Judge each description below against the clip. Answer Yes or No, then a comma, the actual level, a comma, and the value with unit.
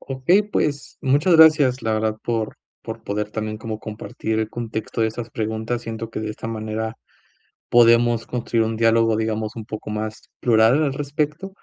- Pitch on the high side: No, low, 115 Hz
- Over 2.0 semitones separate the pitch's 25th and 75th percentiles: Yes, narrow, 2.6 semitones